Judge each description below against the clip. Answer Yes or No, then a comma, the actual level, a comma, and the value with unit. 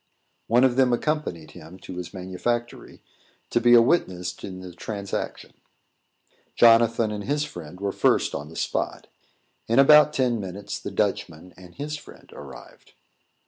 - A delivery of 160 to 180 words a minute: No, average, 150 wpm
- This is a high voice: No, low, 105 Hz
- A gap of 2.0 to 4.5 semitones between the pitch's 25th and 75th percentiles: No, average, 5.2 semitones